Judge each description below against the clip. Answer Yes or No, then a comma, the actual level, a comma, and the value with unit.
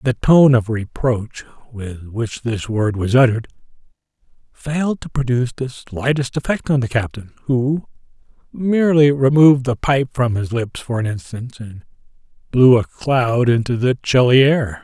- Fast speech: No, average, 155 wpm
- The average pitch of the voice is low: Yes, low, 125 Hz